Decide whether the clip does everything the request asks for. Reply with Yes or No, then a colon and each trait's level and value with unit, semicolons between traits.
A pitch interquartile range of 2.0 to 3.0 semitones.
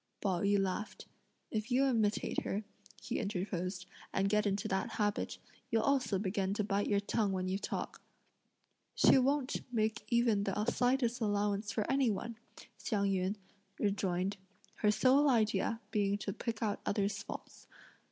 Yes: narrow, 2.5 semitones